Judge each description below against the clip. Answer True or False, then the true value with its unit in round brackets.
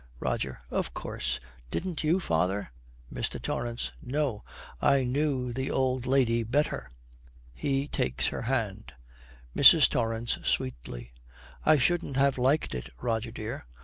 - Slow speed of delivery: True (125 wpm)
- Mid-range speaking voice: False (120 Hz)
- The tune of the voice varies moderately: True (4.9 semitones)